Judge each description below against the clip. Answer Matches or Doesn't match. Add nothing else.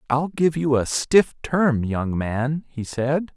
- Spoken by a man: Matches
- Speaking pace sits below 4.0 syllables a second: Matches